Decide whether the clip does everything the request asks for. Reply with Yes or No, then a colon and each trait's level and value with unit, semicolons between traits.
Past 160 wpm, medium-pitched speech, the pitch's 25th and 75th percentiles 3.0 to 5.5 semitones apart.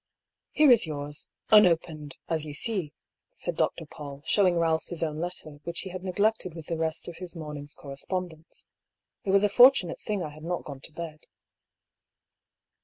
Yes: average, 190 wpm; medium, 165 Hz; average, 3.4 semitones